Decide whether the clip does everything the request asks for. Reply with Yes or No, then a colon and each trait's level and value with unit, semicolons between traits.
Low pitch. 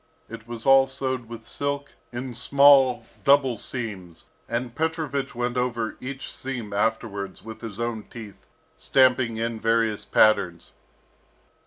Yes: low, 120 Hz